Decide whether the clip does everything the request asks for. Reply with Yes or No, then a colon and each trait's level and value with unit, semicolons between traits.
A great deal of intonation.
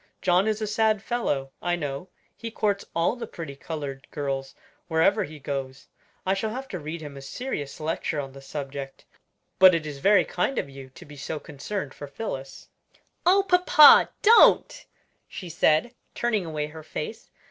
Yes: wide, 7.1 semitones